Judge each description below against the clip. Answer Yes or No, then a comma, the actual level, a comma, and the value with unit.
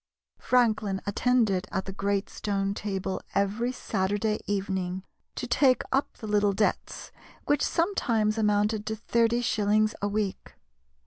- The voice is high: Yes, high, 210 Hz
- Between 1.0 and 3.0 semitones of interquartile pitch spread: Yes, narrow, 2.4 semitones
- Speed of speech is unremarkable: No, slow, 130 wpm